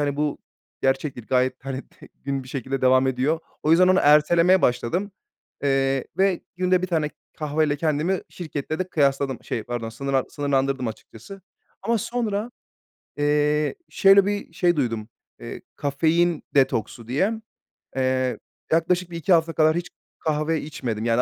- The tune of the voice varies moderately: Yes, average, 4.5 semitones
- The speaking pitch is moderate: Yes, medium, 150 Hz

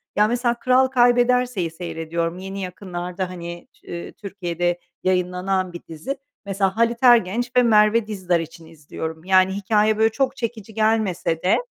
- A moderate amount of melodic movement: Yes, average, 4.5 semitones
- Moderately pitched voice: No, high, 195 Hz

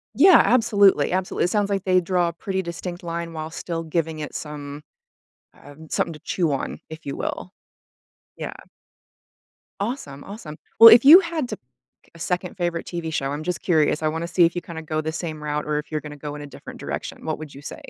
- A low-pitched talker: No, medium, 165 Hz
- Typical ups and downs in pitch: Yes, average, 3.2 semitones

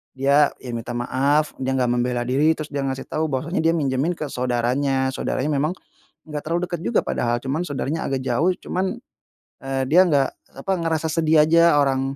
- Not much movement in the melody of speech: No, average, 3.3 semitones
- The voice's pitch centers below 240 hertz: Yes, medium, 140 Hz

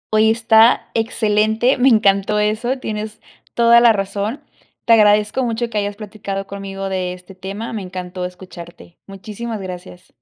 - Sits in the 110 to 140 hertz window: No, high, 210 Hz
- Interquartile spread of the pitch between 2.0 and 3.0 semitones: Yes, narrow, 2.5 semitones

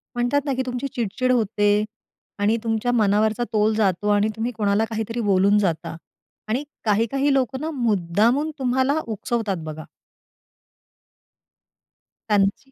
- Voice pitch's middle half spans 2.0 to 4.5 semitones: Yes, average, 3.3 semitones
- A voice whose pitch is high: Yes, high, 220 Hz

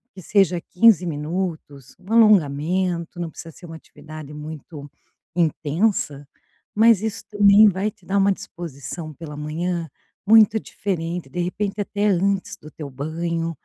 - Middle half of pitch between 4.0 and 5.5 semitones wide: Yes, average, 4.3 semitones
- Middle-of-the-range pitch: Yes, medium, 175 Hz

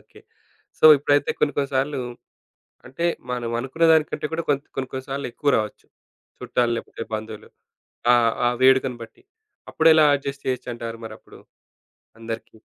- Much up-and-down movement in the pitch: No, average, 3.6 semitones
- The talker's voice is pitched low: Yes, low, 130 Hz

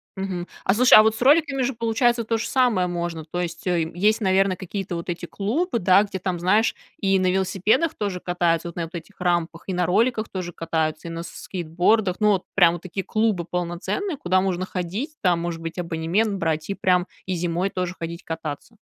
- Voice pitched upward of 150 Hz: Yes, medium, 185 Hz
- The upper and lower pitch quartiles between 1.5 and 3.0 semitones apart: No, average, 3.6 semitones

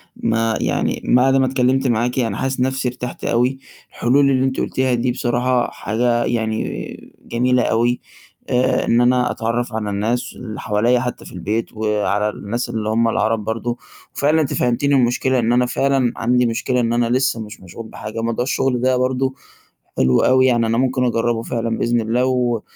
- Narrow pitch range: Yes, narrow, 2.0 semitones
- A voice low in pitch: Yes, low, 120 Hz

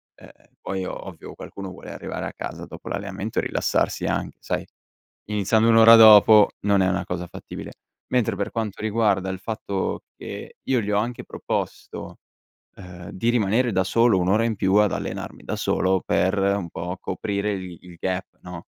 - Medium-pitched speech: No, low, 100 Hz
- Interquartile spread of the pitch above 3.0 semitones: No, average, 2.7 semitones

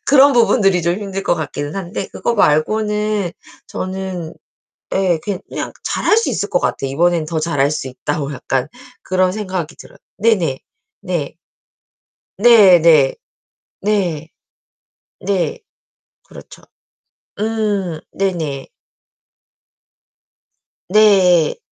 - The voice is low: No, medium, 185 Hz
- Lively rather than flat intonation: No, average, 4.7 semitones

